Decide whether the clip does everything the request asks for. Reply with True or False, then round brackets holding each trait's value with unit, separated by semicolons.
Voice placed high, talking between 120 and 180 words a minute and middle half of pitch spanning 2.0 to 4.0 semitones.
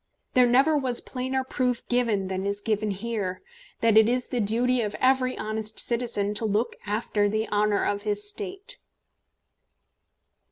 True (225 Hz; 155 wpm; 3.4 semitones)